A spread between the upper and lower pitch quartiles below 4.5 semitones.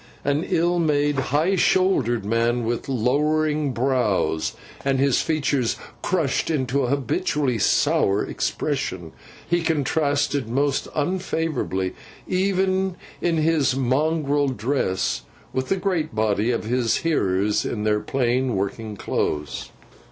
No: average, 5.2 semitones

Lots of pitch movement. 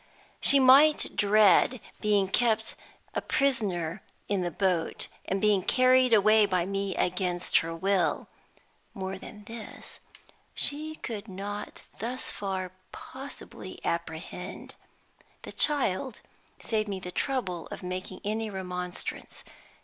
No: average, 4.0 semitones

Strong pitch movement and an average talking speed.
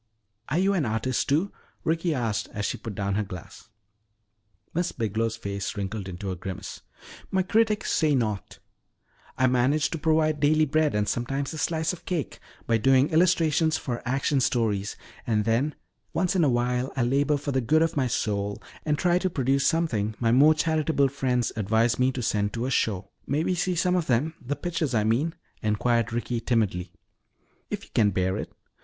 Yes: wide, 5.9 semitones; average, 190 wpm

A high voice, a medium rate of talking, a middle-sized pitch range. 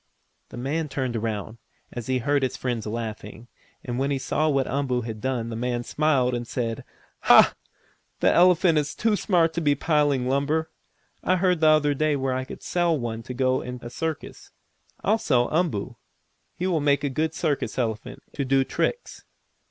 No: low, 135 Hz; average, 185 wpm; average, 4.2 semitones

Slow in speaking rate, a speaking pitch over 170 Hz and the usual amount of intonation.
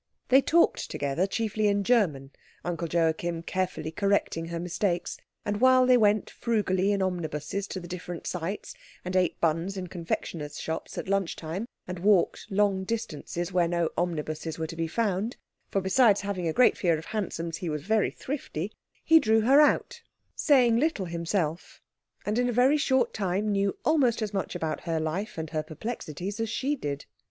No: average, 180 wpm; medium, 185 Hz; average, 4.5 semitones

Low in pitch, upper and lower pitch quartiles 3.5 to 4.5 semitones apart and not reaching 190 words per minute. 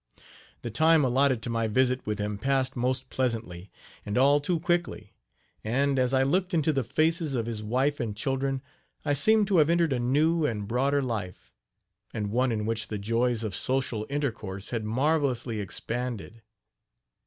Yes: low, 125 Hz; average, 4.2 semitones; average, 170 wpm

